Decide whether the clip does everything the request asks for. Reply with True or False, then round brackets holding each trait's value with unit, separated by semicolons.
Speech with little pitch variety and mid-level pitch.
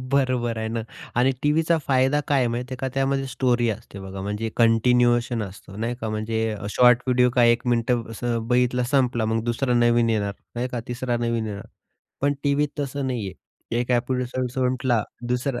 False (2.0 semitones; 120 Hz)